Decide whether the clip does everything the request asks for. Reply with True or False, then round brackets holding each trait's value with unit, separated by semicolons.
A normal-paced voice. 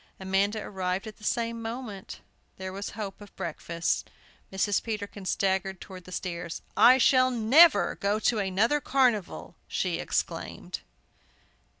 False (130 wpm)